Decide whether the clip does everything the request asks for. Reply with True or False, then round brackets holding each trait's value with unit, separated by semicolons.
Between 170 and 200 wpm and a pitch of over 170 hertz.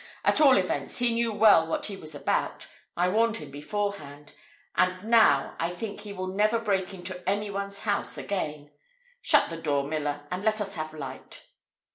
True (185 wpm; 185 Hz)